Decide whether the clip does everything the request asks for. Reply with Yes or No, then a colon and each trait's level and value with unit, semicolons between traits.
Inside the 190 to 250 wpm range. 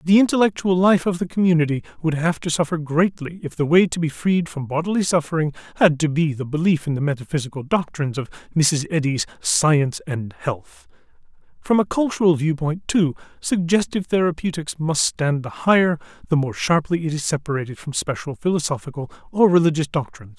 No: average, 170 wpm